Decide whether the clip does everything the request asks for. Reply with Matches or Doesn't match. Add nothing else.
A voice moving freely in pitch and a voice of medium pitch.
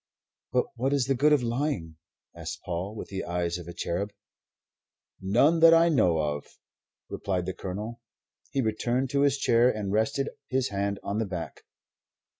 Doesn't match